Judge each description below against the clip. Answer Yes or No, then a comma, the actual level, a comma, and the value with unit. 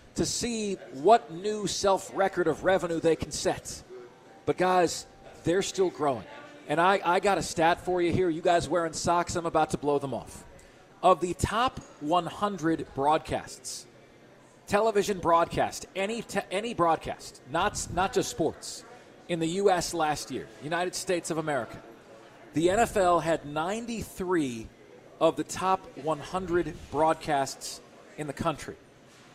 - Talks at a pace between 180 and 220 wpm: No, average, 145 wpm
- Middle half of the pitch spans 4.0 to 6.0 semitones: No, average, 3.3 semitones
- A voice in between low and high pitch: Yes, medium, 175 Hz